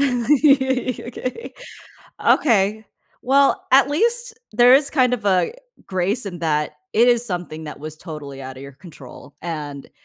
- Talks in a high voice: Yes, high, 215 Hz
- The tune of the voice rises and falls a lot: Yes, wide, 8.9 semitones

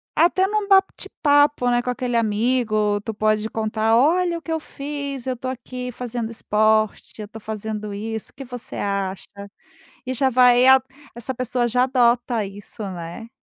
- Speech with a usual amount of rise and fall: Yes, average, 3.3 semitones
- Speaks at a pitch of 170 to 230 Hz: No, high, 240 Hz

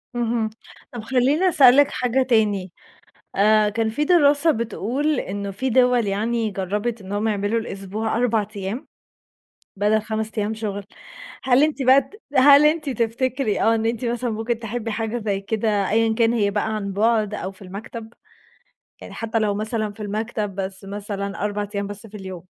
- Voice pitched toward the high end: Yes, high, 220 Hz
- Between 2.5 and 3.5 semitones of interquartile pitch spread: Yes, average, 2.9 semitones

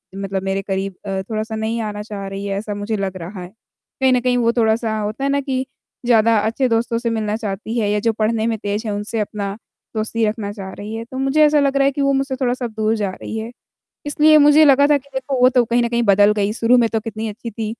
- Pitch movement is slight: No, average, 3.2 semitones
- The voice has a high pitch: Yes, high, 225 Hz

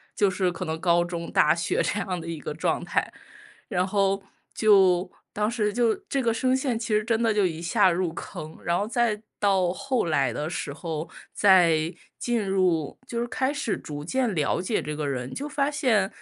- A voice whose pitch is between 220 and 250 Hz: No, high, 190 Hz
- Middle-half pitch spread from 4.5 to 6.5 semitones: Yes, average, 5.2 semitones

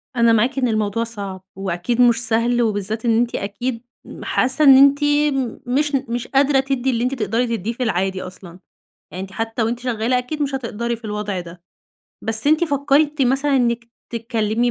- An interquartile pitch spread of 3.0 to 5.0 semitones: Yes, average, 3.6 semitones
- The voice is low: No, high, 235 Hz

